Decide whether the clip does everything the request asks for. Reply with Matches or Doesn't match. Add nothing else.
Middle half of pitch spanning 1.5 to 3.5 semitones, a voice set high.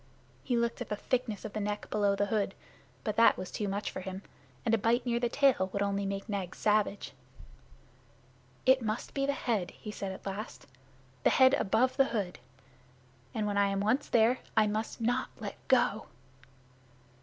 Matches